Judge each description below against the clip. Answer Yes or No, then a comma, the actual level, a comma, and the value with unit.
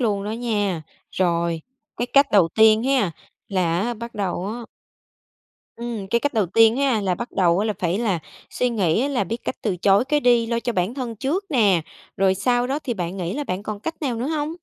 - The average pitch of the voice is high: Yes, high, 220 Hz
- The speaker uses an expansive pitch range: No, average, 4.4 semitones